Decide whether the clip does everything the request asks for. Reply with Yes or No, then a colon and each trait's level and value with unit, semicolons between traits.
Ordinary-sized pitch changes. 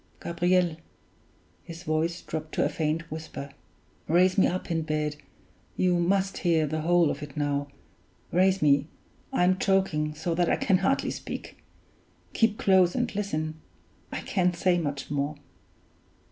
Yes: average, 3.2 semitones